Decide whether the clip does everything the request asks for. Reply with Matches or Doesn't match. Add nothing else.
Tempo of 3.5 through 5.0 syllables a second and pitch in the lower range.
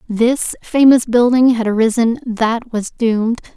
Doesn't match